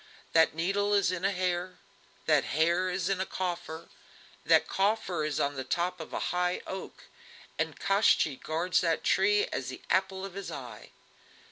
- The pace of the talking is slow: No, average, 170 wpm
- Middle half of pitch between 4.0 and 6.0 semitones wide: No, average, 2.9 semitones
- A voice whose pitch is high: No, medium, 180 Hz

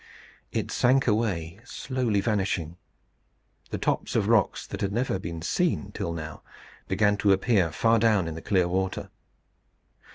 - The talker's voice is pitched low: Yes, low, 100 Hz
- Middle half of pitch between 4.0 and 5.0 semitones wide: Yes, average, 4.7 semitones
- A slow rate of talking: No, average, 150 wpm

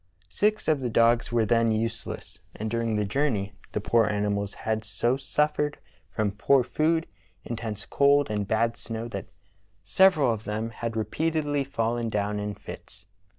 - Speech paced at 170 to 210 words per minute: No, average, 155 wpm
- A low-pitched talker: Yes, low, 115 Hz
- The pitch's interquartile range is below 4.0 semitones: No, average, 4.7 semitones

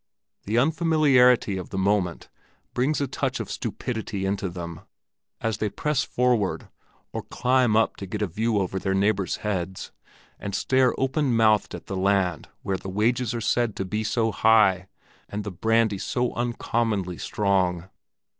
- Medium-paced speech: Yes, average, 160 wpm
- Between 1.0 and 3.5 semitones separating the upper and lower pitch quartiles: No, average, 4.0 semitones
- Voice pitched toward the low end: Yes, low, 105 Hz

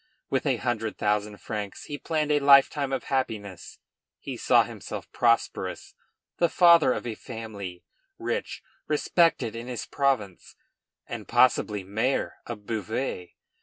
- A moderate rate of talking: No, slow, 130 wpm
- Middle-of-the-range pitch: No, low, 120 Hz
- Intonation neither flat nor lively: Yes, average, 4.7 semitones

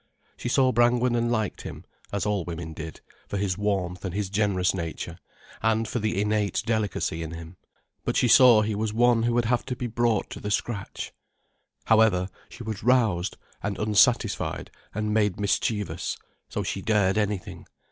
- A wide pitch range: No, average, 3.1 semitones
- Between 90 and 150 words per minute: No, average, 175 wpm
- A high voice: No, low, 105 Hz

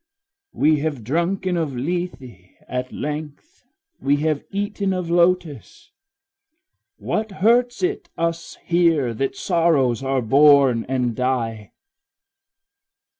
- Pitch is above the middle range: No, medium, 150 Hz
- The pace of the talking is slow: Yes, slow, 105 wpm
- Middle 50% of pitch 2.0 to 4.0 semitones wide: No, wide, 5.4 semitones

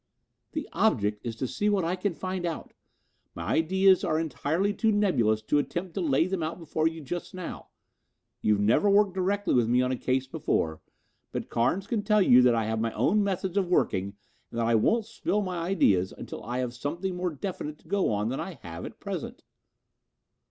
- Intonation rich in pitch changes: Yes, wide, 7.8 semitones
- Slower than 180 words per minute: No, fast, 205 wpm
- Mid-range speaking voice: Yes, medium, 165 Hz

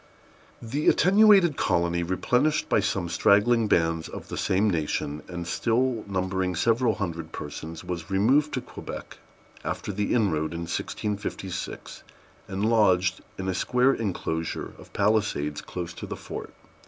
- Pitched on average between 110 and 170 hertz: No, very low, 95 Hz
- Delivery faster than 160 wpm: No, average, 140 wpm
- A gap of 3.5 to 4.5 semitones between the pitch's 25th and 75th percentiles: No, average, 5.1 semitones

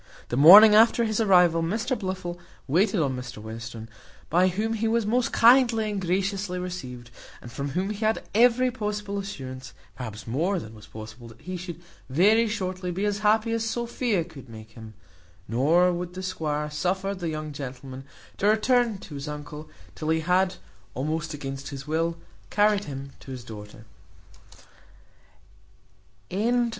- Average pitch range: No, wide, 7.2 semitones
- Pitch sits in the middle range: Yes, medium, 180 Hz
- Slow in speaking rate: No, average, 165 wpm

